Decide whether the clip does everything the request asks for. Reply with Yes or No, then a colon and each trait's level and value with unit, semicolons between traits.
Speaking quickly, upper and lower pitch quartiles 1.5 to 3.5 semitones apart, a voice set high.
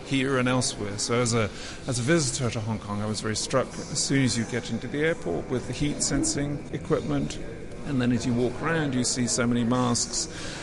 No: fast, 225 wpm; narrow, 2.6 semitones; low, 125 Hz